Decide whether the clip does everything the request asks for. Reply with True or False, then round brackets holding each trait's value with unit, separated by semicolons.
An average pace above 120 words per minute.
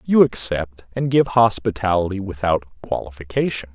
False (110 wpm)